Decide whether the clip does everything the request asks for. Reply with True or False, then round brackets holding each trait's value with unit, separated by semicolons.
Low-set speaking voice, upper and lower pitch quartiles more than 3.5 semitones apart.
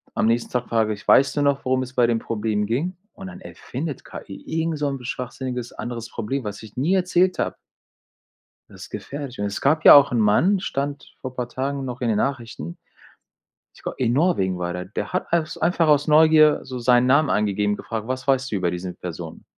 True (130 Hz; 5.0 semitones)